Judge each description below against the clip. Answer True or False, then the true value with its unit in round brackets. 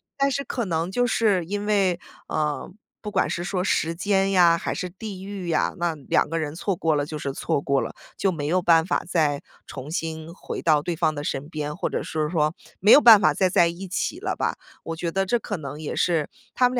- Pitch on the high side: False (170 Hz)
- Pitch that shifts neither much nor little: True (3.9 semitones)